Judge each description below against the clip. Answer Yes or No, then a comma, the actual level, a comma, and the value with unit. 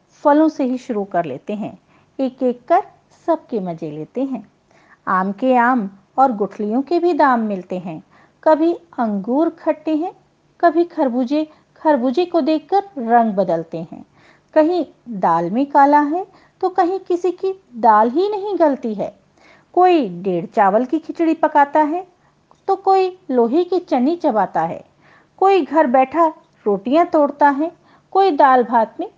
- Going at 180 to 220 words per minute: No, average, 155 wpm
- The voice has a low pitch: No, very high, 290 Hz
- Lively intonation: Yes, wide, 6.5 semitones